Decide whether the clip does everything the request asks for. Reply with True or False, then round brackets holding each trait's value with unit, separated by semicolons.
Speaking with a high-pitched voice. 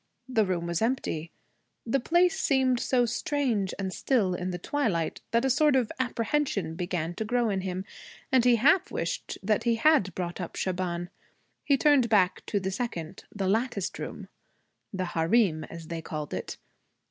True (210 Hz)